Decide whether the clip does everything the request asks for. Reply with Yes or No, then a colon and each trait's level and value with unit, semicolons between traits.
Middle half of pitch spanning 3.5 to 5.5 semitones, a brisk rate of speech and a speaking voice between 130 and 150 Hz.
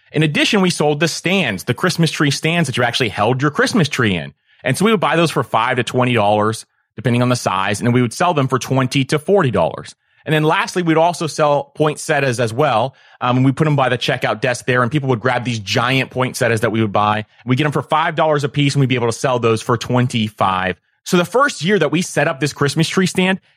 Yes: average, 4.6 semitones; fast, 265 wpm; medium, 140 Hz